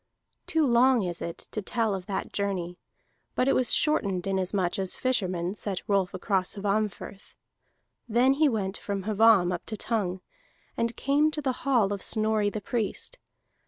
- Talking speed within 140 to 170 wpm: Yes, average, 160 wpm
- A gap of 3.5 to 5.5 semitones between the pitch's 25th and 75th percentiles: Yes, average, 4.0 semitones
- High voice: Yes, high, 205 Hz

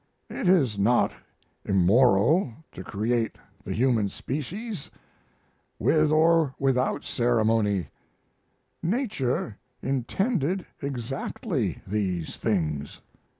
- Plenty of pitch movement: Yes, wide, 6.8 semitones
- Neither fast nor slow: No, slow, 80 wpm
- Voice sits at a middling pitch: No, low, 125 Hz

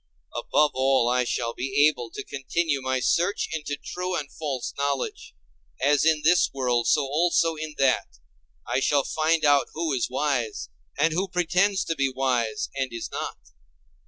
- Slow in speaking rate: No, average, 165 wpm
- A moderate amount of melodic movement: Yes, average, 3.5 semitones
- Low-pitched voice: No, medium, 145 Hz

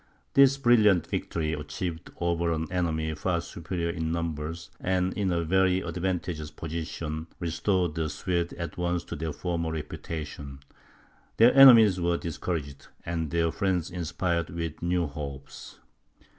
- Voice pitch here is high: No, very low, 85 Hz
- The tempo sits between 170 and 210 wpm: No, slow, 135 wpm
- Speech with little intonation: Yes, narrow, 2.2 semitones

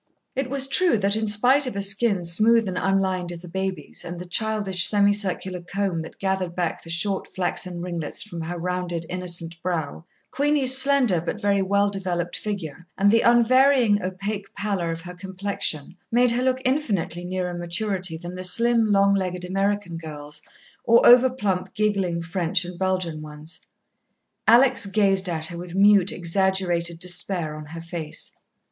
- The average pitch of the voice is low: No, high, 190 Hz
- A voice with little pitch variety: No, average, 3.2 semitones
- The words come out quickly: No, average, 165 wpm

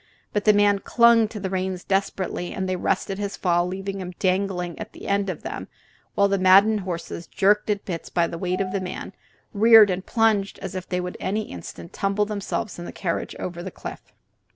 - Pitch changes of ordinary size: No, narrow, 2.1 semitones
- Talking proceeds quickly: Yes, fast, 220 wpm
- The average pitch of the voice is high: Yes, high, 195 Hz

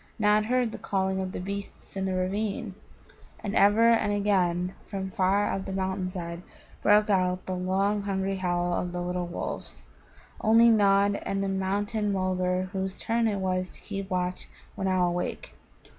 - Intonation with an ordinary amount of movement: No, narrow, 1.9 semitones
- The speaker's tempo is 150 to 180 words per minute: Yes, average, 175 wpm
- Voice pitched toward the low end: No, high, 190 Hz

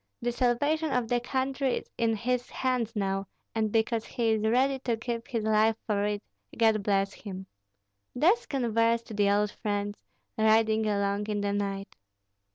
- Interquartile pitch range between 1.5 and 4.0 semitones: Yes, average, 3.0 semitones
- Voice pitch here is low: No, high, 225 Hz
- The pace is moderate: Yes, average, 165 wpm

